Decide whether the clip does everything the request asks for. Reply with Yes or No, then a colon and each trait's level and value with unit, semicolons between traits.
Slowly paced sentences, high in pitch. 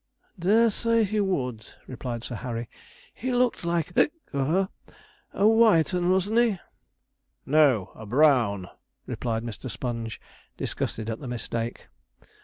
No: slow, 130 wpm; medium, 145 Hz